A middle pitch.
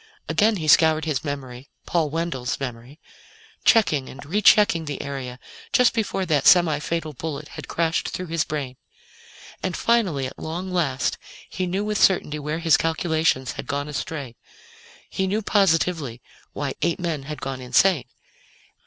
Yes: medium, 160 Hz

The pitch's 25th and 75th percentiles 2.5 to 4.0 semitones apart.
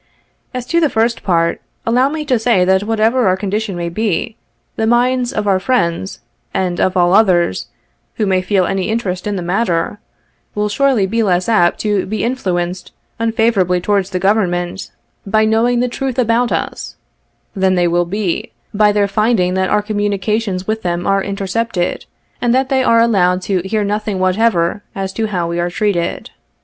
Yes: average, 3.7 semitones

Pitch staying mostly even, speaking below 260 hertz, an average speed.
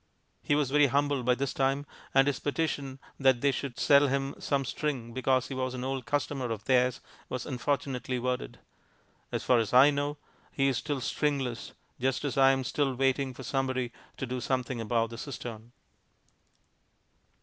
Yes: narrow, 1.9 semitones; low, 135 Hz; average, 175 wpm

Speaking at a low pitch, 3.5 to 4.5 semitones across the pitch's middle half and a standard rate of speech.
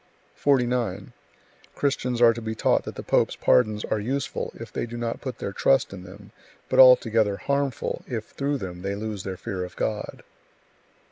Yes: low, 115 Hz; average, 4.1 semitones; average, 180 wpm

